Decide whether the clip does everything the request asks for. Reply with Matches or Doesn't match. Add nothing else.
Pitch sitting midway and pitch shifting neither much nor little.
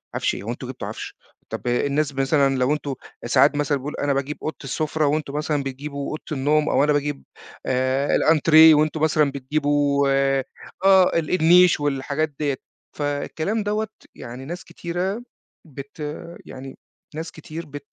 Doesn't match